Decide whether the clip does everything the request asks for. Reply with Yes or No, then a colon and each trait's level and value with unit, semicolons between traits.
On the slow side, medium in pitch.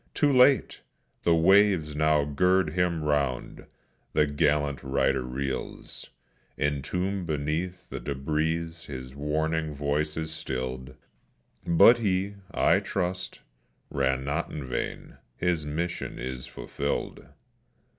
No: slow, 110 wpm; very low, 75 Hz